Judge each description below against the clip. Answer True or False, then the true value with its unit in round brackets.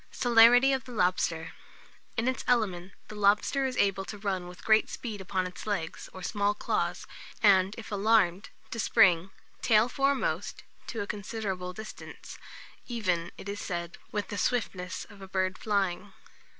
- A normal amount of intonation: True (3.3 semitones)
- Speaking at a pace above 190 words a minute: False (160 wpm)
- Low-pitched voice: False (205 Hz)